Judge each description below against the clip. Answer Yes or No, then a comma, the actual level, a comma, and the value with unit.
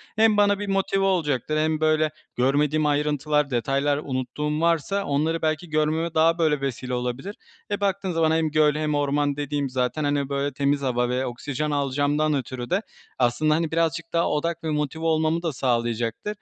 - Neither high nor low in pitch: Yes, medium, 150 Hz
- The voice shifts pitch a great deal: No, average, 2.8 semitones